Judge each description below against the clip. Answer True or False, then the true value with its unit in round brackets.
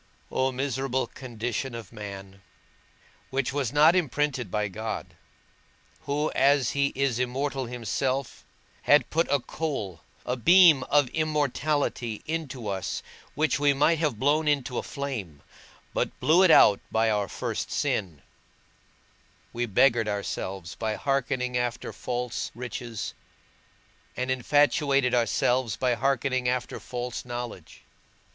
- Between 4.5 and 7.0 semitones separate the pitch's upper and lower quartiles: False (3.6 semitones)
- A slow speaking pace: True (125 wpm)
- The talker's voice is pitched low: True (125 Hz)